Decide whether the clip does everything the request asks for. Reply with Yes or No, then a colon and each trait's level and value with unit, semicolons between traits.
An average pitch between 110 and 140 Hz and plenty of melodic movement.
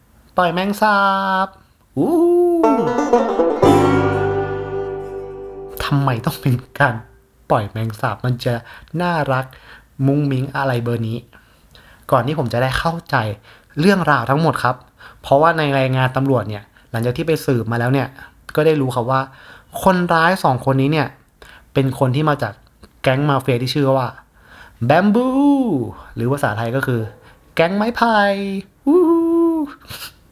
Yes: low, 135 Hz; wide, 6.1 semitones